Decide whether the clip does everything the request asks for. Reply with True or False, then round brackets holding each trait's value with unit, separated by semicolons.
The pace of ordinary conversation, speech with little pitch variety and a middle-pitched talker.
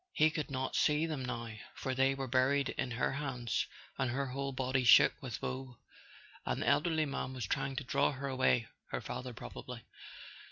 False (185 wpm; 1.6 semitones; 130 Hz)